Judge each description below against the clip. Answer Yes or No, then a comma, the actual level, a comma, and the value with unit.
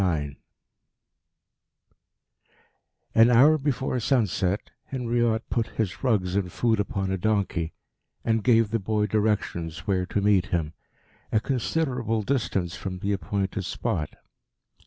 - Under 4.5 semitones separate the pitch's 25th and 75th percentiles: Yes, average, 4.0 semitones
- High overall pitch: No, low, 105 Hz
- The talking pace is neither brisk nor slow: No, slow, 120 wpm